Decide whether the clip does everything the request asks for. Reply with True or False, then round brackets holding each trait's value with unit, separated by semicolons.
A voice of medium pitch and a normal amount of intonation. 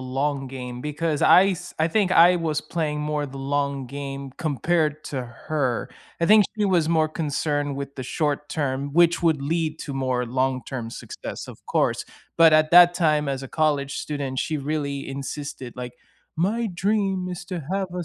True (150 Hz; 3.5 semitones)